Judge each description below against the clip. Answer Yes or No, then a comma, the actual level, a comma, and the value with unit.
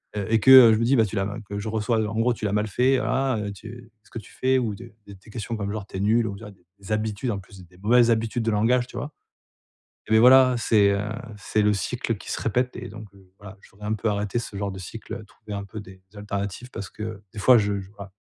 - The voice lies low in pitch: Yes, low, 110 Hz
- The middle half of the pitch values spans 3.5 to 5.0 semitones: No, average, 2.7 semitones